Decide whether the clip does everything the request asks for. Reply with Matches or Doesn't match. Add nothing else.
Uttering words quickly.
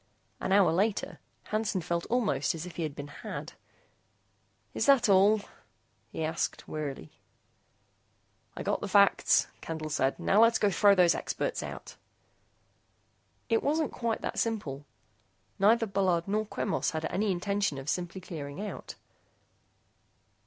Doesn't match